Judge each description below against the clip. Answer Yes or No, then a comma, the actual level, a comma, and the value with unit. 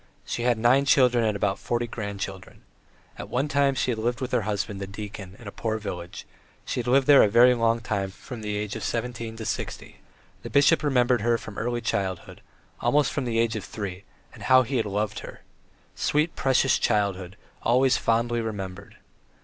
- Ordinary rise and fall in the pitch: Yes, average, 3.3 semitones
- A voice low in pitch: Yes, low, 115 Hz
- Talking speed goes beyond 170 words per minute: Yes, average, 195 wpm